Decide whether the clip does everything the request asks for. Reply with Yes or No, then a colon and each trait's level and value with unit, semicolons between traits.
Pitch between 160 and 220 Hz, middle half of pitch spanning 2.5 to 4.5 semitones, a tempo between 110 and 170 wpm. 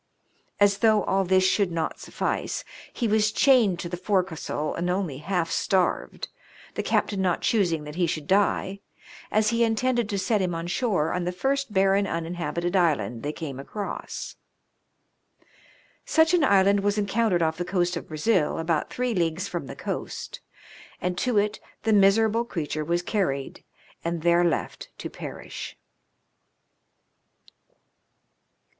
Yes: high, 190 Hz; average, 3.8 semitones; average, 150 wpm